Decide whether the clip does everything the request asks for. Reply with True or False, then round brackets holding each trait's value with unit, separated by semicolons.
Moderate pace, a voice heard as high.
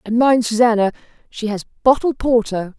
True (150 wpm; 230 Hz)